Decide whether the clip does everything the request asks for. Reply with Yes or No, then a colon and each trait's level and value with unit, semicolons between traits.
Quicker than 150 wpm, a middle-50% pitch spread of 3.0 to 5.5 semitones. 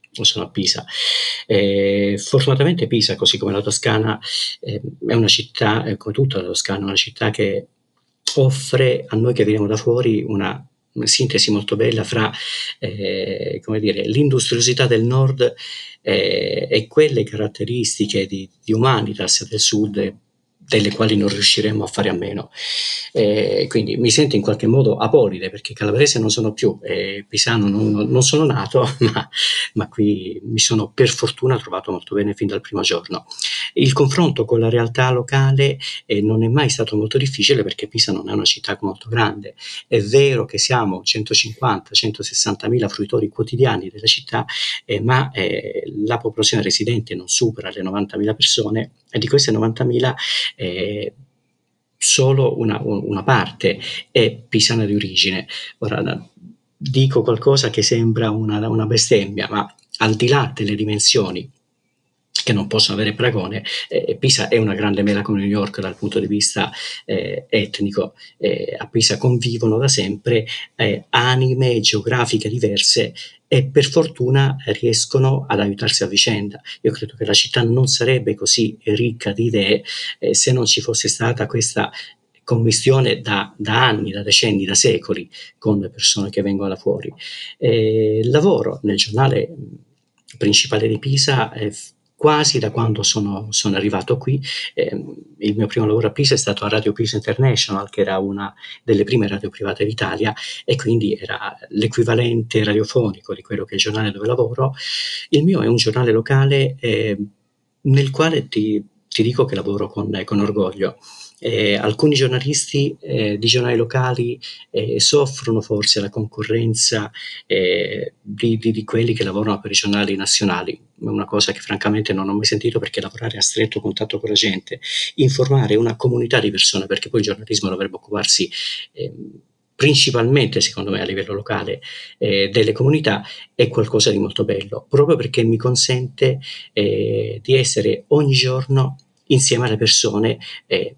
Yes: average, 160 wpm; average, 4.1 semitones